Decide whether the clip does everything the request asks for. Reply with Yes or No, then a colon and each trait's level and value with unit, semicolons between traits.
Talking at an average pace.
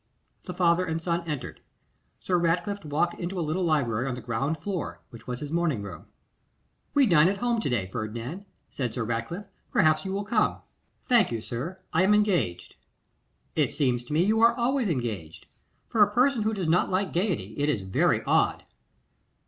Yes: average, 190 wpm